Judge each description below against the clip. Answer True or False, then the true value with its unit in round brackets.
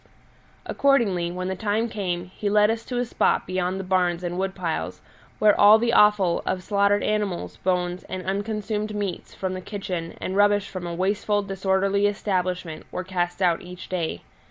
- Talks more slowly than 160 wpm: False (180 wpm)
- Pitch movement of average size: False (2.3 semitones)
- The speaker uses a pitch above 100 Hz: True (190 Hz)